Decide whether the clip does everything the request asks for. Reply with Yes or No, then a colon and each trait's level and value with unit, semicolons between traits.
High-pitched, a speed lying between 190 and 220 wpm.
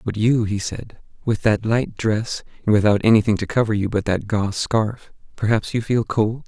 No: low, 110 Hz; fast, 205 wpm